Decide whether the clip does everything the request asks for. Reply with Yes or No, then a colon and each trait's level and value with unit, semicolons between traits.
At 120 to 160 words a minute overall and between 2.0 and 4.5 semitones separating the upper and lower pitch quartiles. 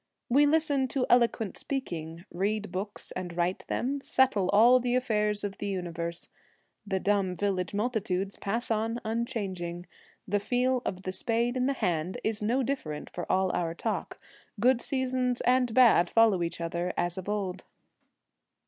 No: average, 155 wpm; average, 5.3 semitones